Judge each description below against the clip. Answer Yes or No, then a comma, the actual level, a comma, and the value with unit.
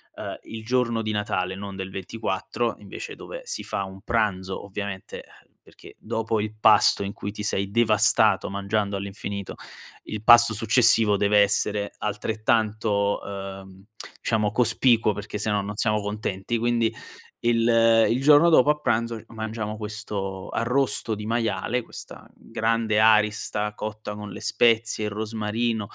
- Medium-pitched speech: No, low, 110 Hz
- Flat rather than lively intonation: Yes, narrow, 2.1 semitones